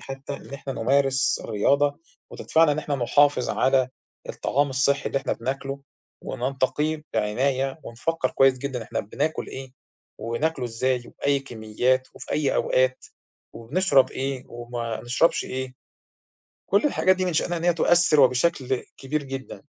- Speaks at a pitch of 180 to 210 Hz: No, low, 135 Hz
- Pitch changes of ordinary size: No, narrow, 2.3 semitones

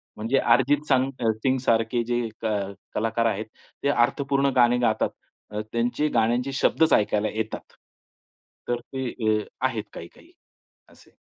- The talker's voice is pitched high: No, low, 120 Hz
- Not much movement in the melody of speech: No, average, 3.1 semitones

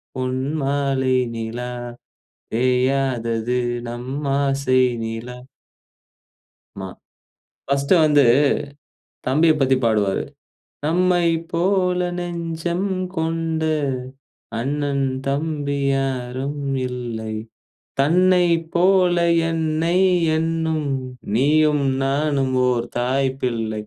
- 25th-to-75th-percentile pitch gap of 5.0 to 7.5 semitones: No, average, 4.3 semitones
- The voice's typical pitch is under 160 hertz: Yes, medium, 140 Hz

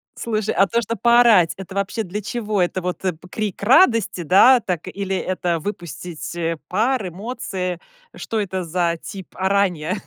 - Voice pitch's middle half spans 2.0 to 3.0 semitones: No, average, 3.4 semitones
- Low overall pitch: No, high, 190 Hz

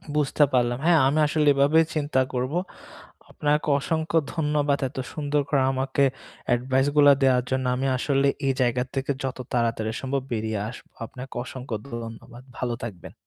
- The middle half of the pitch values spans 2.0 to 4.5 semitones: Yes, average, 2.7 semitones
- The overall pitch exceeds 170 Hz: No, low, 135 Hz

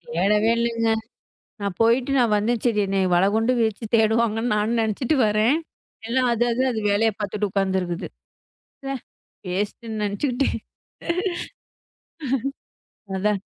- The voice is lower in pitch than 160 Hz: No, high, 220 Hz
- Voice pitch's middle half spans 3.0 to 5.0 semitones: No, narrow, 2.4 semitones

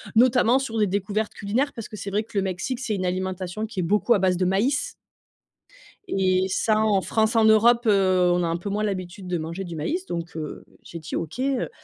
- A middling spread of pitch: Yes, average, 3.4 semitones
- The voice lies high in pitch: Yes, high, 200 Hz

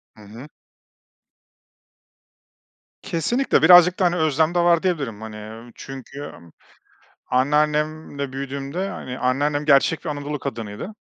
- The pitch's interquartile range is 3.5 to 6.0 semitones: Yes, average, 4.3 semitones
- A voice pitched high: No, medium, 145 Hz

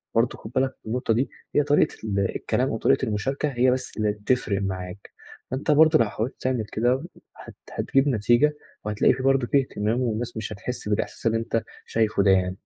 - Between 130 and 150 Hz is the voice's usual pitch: No, low, 115 Hz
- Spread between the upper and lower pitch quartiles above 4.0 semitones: No, average, 3.7 semitones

